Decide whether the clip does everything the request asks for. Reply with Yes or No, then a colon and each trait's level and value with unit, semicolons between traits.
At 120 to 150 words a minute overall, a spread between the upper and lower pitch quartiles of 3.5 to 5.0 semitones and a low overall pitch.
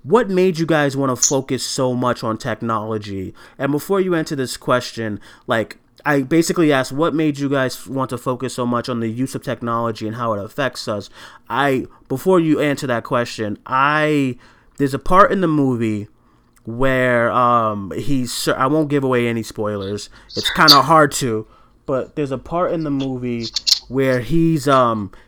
No: average, 185 wpm; average, 3.8 semitones; low, 130 Hz